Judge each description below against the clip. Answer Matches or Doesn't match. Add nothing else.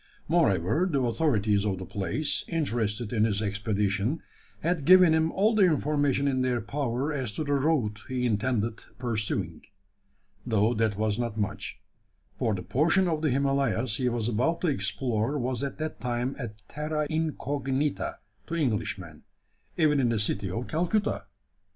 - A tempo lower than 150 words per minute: Doesn't match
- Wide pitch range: Matches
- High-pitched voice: Doesn't match